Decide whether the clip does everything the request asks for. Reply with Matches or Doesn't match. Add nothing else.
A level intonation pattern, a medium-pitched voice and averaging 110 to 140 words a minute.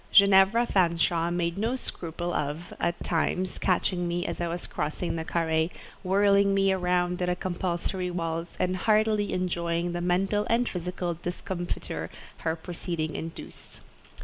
Matches